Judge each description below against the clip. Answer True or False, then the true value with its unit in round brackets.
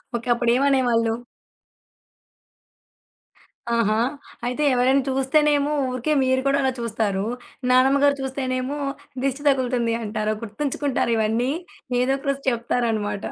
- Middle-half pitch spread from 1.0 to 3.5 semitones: True (2.9 semitones)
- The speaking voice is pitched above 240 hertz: True (255 Hz)